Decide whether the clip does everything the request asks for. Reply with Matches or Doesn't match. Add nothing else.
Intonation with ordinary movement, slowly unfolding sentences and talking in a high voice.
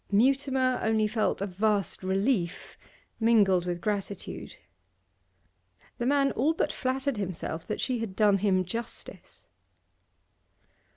Matches